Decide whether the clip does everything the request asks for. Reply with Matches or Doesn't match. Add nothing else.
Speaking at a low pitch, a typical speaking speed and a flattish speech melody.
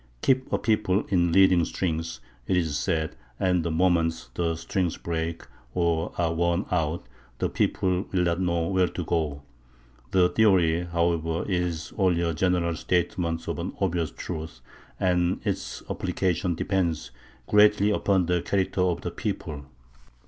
Matches